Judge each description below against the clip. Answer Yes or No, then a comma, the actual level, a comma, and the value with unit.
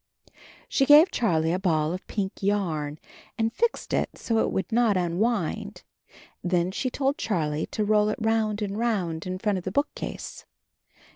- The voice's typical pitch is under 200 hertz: No, high, 205 Hz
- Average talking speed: Yes, average, 170 wpm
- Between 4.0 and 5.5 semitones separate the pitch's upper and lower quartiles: Yes, average, 4.3 semitones